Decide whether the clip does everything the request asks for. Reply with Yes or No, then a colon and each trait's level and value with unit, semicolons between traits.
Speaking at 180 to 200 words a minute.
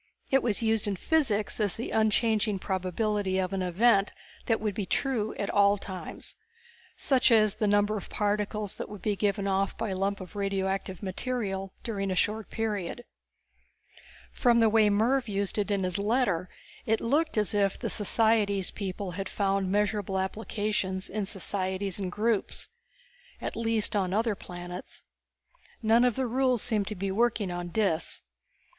No: average, 165 wpm